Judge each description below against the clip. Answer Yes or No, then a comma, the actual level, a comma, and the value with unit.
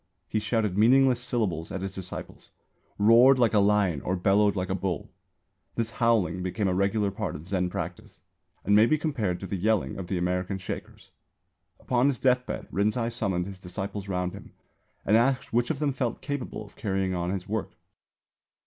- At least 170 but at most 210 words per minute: Yes, average, 185 wpm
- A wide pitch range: No, average, 3.9 semitones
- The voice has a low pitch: Yes, low, 100 Hz